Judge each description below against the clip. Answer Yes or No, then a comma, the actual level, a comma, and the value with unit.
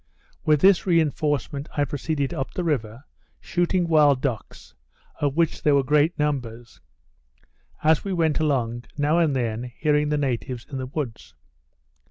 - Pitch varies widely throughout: No, average, 3.4 semitones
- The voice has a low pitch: No, medium, 145 Hz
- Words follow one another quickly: No, average, 150 wpm